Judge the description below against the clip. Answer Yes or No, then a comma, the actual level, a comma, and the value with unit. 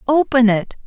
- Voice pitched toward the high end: Yes, high, 245 Hz